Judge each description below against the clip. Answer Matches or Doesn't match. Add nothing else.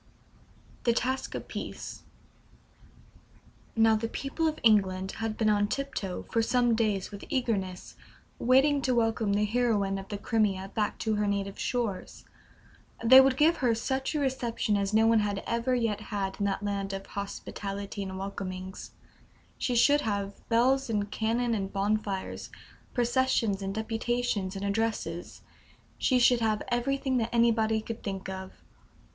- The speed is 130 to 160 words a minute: Matches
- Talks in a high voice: Matches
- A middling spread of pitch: Matches